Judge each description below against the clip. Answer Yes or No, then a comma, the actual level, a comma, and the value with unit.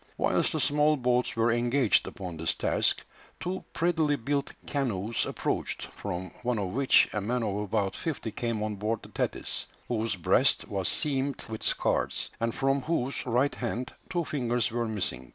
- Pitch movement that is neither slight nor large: Yes, average, 4.6 semitones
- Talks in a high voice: No, low, 120 Hz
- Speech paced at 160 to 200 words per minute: Yes, average, 170 wpm